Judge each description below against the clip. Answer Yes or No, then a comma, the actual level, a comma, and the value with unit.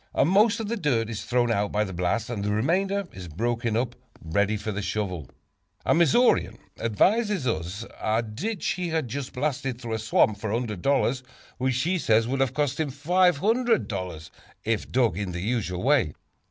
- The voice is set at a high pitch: No, low, 120 Hz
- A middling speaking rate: Yes, average, 180 wpm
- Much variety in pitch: Yes, wide, 6.3 semitones